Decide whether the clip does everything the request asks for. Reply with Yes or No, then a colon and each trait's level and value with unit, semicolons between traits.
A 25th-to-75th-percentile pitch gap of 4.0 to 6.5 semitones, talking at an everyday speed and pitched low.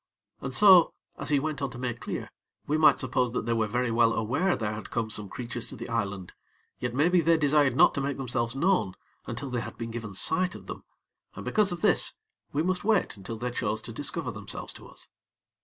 No: average, 5.1 semitones; fast, 225 wpm; low, 125 Hz